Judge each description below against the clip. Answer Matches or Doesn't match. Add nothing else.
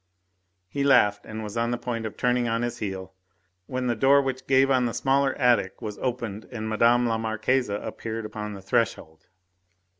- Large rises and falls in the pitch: Doesn't match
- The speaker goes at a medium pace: Matches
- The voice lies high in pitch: Doesn't match